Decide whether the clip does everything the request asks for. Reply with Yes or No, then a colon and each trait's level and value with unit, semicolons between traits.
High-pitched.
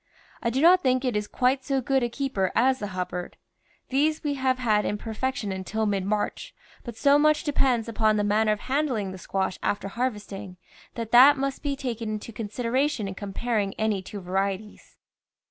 Yes: high, 230 Hz